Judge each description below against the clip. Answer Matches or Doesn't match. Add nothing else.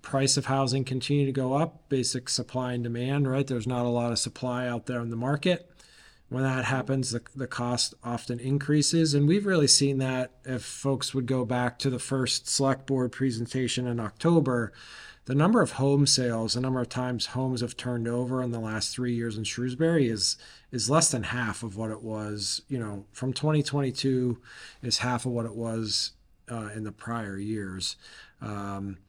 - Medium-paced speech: Matches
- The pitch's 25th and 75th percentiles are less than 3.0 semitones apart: Matches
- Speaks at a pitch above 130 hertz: Doesn't match